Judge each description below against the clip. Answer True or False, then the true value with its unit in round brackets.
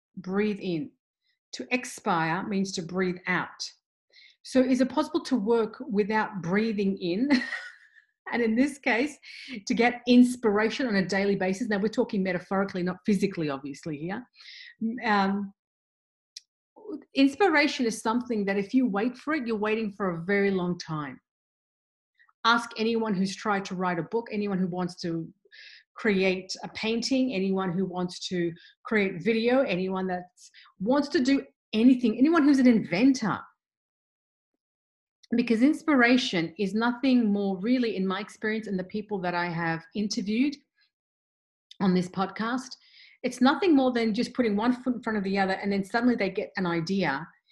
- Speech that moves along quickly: False (155 wpm)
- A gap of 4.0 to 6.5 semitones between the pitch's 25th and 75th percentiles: True (4.7 semitones)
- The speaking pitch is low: False (215 Hz)